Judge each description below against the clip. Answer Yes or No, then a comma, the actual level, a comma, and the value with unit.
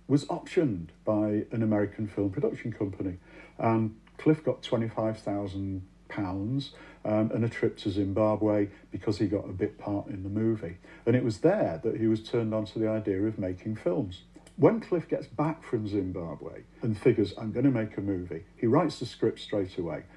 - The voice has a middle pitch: No, low, 110 Hz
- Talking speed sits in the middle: Yes, average, 190 wpm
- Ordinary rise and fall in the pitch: No, narrow, 2.3 semitones